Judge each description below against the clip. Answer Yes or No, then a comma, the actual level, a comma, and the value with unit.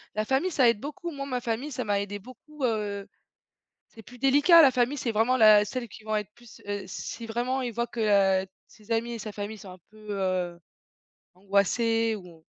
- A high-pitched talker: Yes, high, 225 Hz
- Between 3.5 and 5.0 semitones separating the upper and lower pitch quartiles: Yes, average, 3.8 semitones